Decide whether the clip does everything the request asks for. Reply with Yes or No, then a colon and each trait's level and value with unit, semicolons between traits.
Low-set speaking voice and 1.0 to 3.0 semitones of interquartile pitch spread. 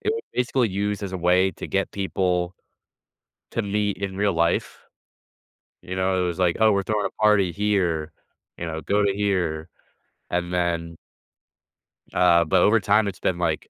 Yes: very low, 95 Hz; average, 2.7 semitones